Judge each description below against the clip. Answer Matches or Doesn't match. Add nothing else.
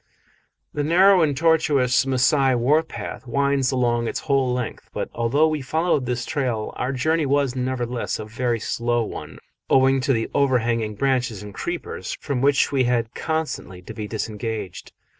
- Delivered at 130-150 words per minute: Doesn't match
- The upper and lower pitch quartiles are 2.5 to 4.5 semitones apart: Matches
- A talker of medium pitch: Doesn't match